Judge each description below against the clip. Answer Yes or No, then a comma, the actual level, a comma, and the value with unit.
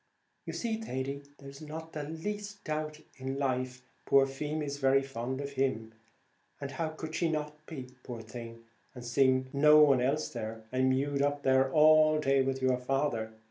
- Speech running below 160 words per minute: No, average, 175 wpm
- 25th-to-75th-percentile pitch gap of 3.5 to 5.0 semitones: No, average, 2.7 semitones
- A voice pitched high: No, low, 135 Hz